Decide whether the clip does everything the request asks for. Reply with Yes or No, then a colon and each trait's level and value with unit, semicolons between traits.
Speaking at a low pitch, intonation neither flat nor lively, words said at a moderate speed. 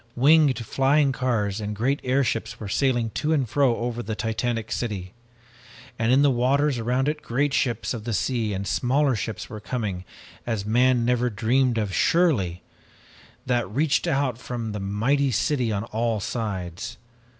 Yes: low, 120 Hz; average, 3.6 semitones; average, 160 wpm